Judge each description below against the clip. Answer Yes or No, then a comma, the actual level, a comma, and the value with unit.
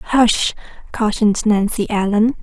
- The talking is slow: Yes, slow, 100 wpm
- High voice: Yes, high, 215 Hz